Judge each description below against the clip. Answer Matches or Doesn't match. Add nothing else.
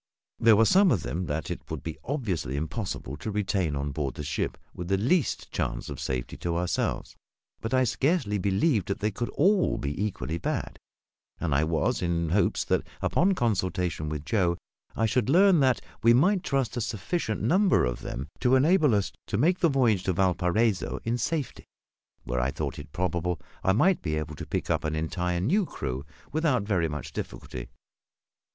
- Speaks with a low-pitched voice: Matches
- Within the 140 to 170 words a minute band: Doesn't match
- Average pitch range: Doesn't match